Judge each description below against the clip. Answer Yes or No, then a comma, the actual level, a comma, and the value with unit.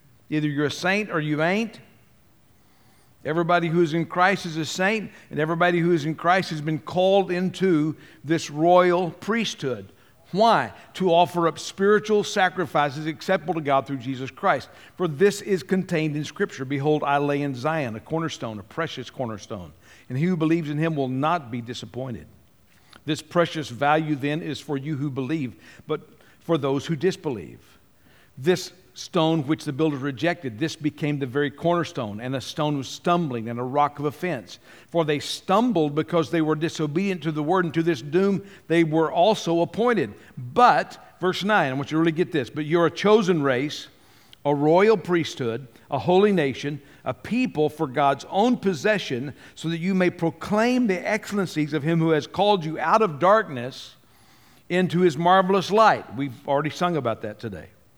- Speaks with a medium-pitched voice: Yes, medium, 160 Hz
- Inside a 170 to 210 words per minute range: Yes, average, 180 wpm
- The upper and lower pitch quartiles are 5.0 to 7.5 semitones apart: No, average, 4.3 semitones